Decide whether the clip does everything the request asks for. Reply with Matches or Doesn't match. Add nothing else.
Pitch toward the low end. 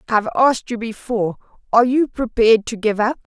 Doesn't match